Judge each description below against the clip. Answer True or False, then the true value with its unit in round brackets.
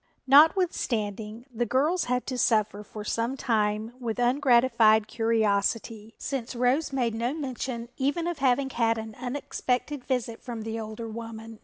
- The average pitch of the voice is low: False (235 Hz)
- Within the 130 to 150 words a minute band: True (145 wpm)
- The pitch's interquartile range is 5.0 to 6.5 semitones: False (2.9 semitones)